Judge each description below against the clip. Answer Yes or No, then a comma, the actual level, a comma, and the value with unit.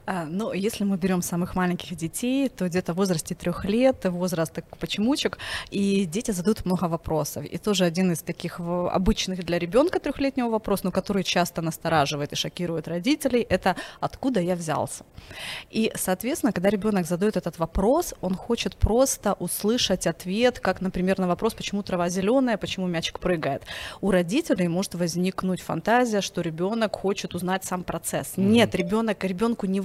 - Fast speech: Yes, fast, 160 wpm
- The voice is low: No, high, 190 Hz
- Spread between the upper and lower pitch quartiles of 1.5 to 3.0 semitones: No, average, 3.6 semitones